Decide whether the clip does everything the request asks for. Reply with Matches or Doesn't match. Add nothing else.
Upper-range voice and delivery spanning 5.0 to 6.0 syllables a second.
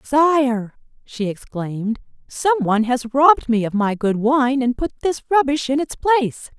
Doesn't match